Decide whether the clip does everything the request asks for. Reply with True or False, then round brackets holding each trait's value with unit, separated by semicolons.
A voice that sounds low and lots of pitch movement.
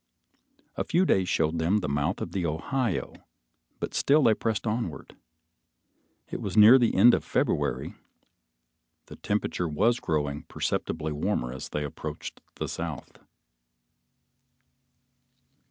True (90 Hz; 6.6 semitones)